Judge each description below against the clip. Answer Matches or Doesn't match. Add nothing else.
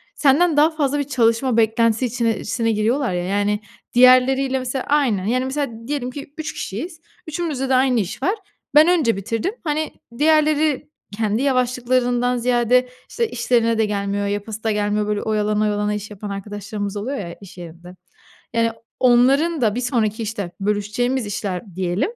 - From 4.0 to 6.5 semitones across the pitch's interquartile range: Matches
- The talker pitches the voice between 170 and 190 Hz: Doesn't match